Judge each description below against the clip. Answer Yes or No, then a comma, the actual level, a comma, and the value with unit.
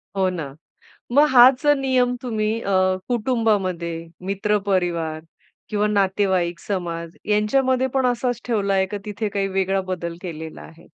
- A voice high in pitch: Yes, high, 205 Hz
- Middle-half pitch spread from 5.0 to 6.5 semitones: Yes, average, 5.3 semitones